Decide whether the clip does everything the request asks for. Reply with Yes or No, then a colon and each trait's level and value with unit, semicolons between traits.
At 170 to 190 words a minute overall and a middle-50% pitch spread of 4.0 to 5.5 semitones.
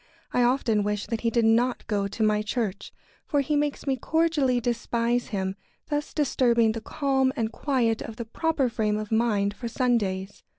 No: average, 180 wpm; average, 3.4 semitones